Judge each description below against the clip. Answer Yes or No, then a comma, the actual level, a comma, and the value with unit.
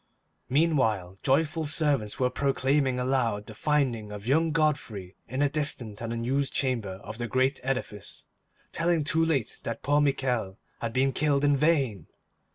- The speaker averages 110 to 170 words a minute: Yes, average, 155 wpm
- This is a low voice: Yes, low, 130 Hz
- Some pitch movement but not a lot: Yes, average, 4.3 semitones